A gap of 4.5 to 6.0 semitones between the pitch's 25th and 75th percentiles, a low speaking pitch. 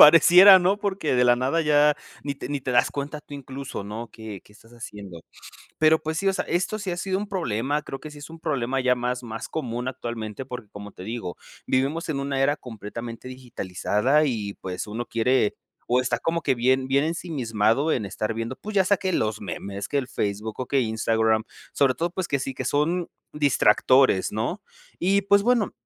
Yes: wide, 5.6 semitones; low, 130 Hz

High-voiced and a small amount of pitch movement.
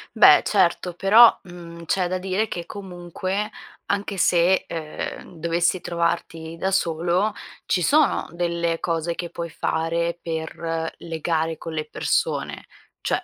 No: medium, 170 Hz; narrow, 1.9 semitones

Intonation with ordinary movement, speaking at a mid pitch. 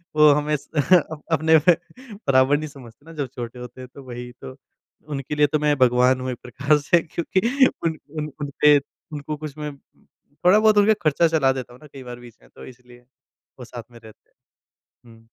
Yes: average, 3.7 semitones; medium, 145 Hz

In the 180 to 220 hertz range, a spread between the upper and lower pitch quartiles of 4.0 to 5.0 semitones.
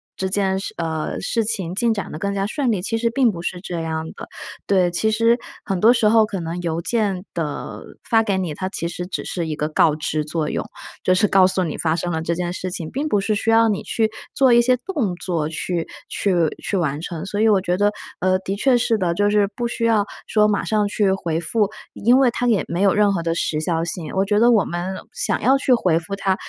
Yes: high, 195 Hz; average, 4.4 semitones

